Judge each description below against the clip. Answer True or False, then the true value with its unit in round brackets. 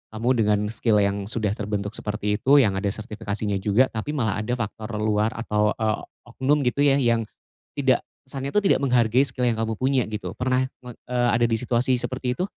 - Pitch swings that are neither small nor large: True (3.2 semitones)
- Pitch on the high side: False (115 Hz)